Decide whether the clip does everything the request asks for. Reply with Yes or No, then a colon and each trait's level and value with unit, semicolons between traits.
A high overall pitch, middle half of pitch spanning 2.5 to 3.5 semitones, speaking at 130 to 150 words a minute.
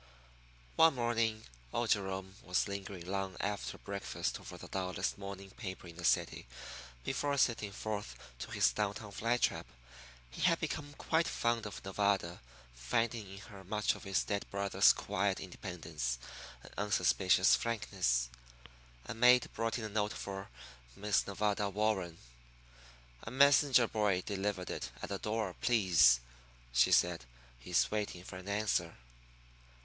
No: low, 100 Hz; average, 3.2 semitones; average, 145 wpm